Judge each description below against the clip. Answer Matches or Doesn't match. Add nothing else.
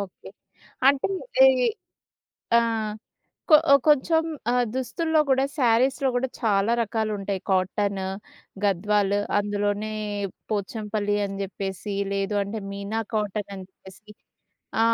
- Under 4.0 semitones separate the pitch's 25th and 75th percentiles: Matches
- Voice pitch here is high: Matches